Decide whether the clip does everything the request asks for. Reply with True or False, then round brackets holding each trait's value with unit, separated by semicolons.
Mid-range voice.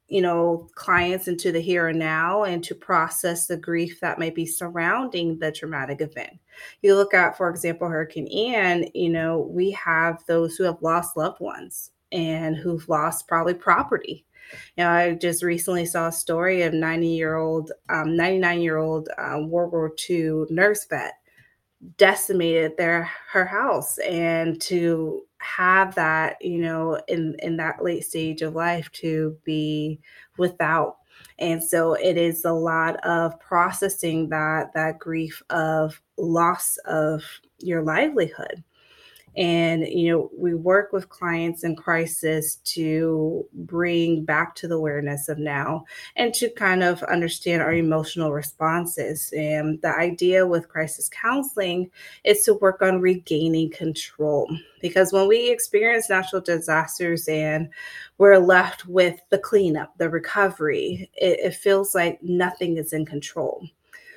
True (170 Hz)